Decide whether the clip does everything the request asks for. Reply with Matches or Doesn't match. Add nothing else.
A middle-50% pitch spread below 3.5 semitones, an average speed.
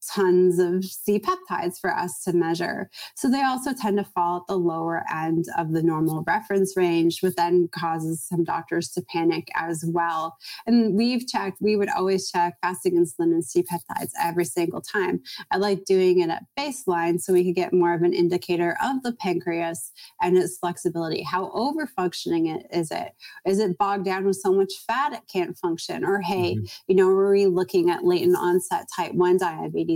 Matches